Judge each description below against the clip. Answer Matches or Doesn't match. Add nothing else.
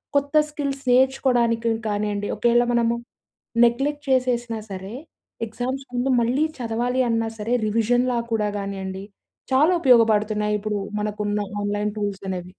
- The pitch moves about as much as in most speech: Matches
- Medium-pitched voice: Doesn't match